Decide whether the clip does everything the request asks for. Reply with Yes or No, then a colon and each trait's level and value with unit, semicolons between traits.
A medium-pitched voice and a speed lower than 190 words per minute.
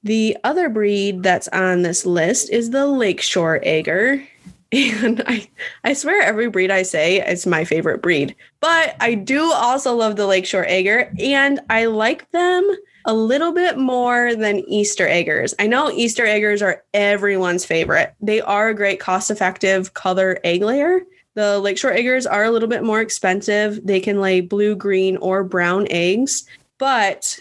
No: high, 210 Hz; average, 165 wpm